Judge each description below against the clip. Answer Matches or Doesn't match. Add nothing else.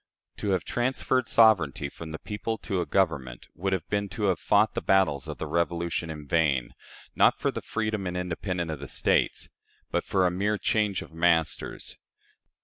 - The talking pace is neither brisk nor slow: Matches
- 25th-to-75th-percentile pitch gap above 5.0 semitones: Doesn't match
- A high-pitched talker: Doesn't match